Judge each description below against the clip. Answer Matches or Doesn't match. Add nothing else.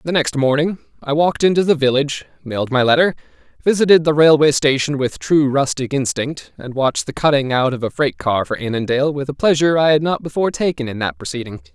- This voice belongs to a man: Matches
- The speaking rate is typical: Doesn't match